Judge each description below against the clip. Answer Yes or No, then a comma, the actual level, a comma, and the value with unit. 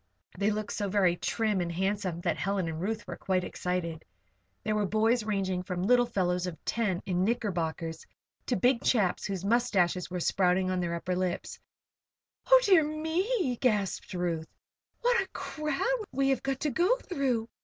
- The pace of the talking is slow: No, average, 175 wpm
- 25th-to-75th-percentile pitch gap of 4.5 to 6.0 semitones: Yes, wide, 5.6 semitones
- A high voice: Yes, high, 200 Hz